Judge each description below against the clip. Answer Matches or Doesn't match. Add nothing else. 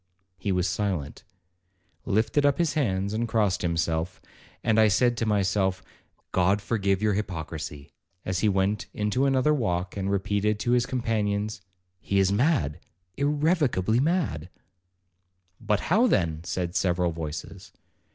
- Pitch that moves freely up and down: Doesn't match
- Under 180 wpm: Matches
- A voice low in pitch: Matches